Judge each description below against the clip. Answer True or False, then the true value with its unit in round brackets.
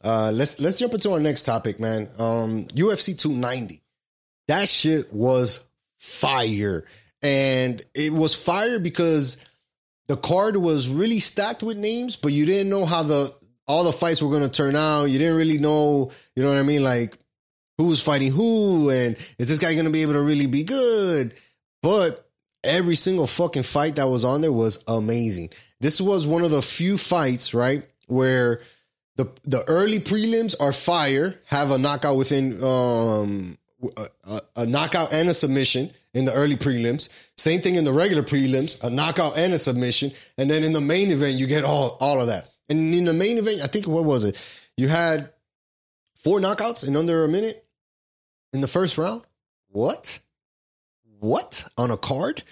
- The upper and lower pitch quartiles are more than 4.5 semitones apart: True (5.1 semitones)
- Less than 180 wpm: False (185 wpm)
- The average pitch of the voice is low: False (145 Hz)